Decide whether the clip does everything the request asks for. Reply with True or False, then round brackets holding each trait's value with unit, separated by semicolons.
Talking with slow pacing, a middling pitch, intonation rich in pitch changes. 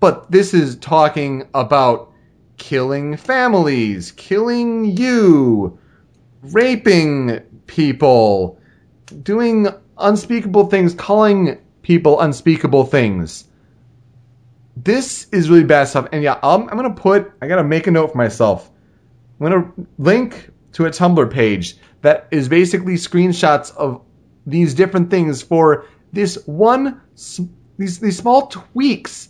True (120 wpm; 170 Hz; 6.6 semitones)